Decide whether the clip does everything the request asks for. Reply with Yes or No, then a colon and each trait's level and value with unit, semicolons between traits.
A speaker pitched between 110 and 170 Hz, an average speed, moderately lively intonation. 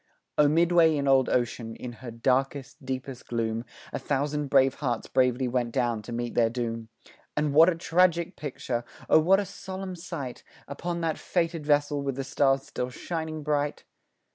Yes: medium, 140 Hz; average, 170 wpm; average, 4.4 semitones